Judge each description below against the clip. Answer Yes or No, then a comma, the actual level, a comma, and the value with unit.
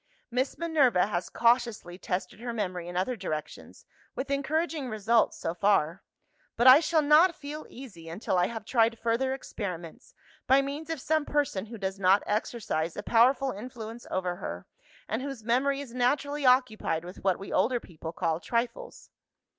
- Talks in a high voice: Yes, high, 235 Hz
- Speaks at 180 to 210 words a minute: No, average, 165 wpm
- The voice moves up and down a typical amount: No, wide, 6.1 semitones